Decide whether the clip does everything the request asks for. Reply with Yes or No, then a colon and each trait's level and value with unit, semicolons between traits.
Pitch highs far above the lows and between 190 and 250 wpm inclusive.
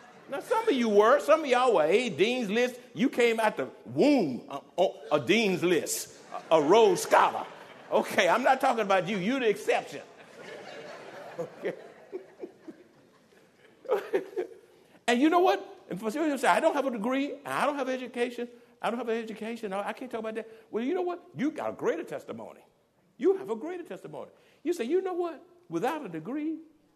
Yes: wide, 7.4 semitones; average, 200 wpm